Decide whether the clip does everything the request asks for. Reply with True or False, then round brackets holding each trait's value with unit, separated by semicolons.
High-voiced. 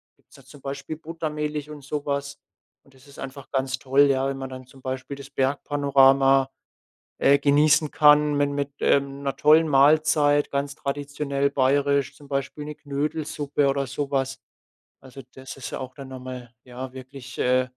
False (140 Hz)